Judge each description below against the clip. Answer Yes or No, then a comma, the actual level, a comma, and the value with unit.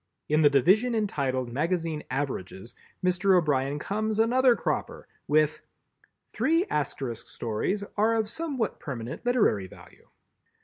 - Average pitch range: No, wide, 8.3 semitones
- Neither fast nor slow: No, slow, 120 wpm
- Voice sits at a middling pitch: Yes, medium, 160 Hz